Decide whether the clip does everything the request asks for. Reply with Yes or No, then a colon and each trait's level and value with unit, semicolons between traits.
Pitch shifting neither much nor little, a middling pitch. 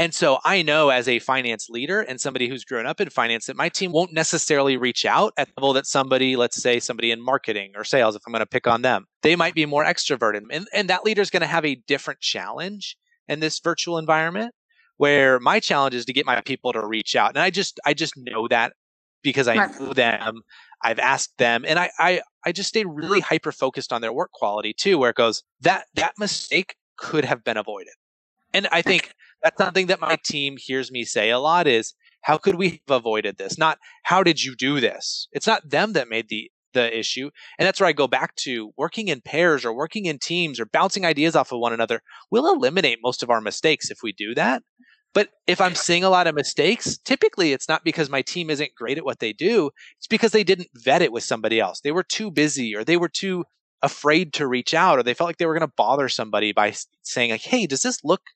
No: wide, 5.8 semitones; medium, 145 Hz